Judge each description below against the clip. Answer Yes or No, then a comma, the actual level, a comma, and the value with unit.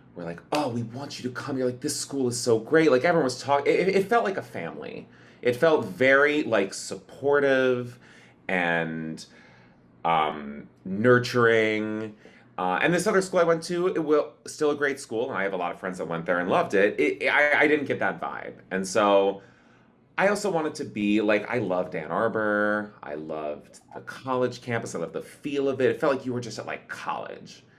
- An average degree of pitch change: No, wide, 5.9 semitones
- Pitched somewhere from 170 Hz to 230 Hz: No, low, 125 Hz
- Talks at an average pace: No, fast, 215 wpm